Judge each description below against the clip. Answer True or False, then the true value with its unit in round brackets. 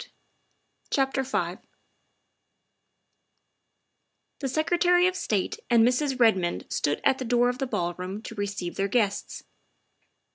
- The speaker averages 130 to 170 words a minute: True (135 wpm)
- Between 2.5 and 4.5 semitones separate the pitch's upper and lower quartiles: False (5.1 semitones)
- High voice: True (240 Hz)